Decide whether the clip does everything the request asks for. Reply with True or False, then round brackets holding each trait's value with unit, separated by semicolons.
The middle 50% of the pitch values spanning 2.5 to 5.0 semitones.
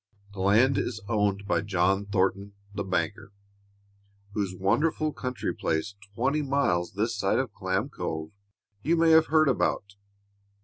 False (5.4 semitones)